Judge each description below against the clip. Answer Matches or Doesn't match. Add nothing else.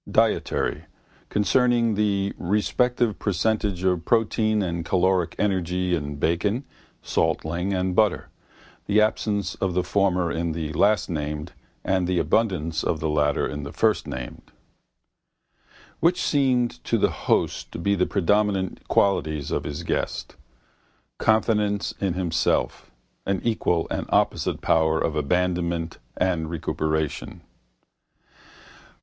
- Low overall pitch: Matches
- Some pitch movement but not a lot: Matches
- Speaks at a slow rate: Matches